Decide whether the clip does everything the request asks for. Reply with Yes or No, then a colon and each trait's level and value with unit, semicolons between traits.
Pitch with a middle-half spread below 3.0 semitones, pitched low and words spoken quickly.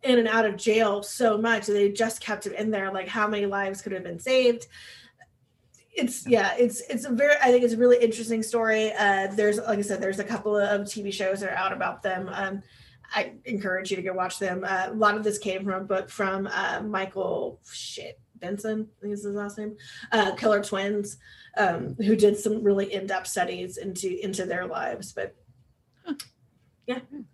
No: narrow, 2.6 semitones; high, 205 Hz; fast, 210 wpm